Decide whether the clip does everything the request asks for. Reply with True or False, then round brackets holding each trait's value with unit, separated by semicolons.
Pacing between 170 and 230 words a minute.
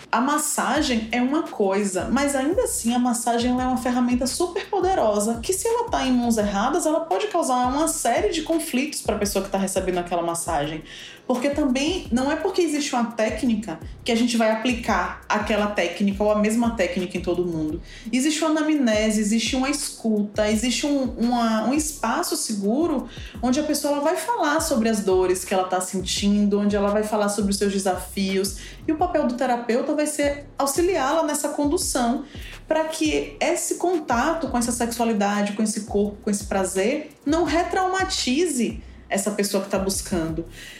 True (180 wpm)